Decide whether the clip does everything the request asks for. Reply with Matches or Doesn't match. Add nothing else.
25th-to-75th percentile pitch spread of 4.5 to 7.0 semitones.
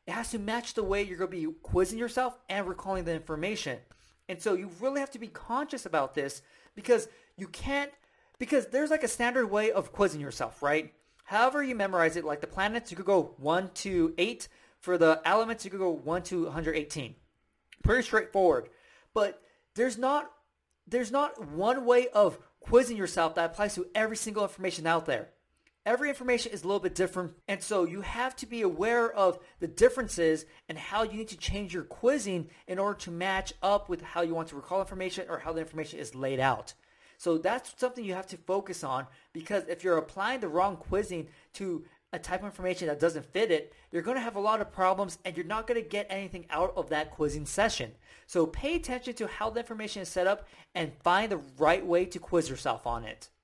Matches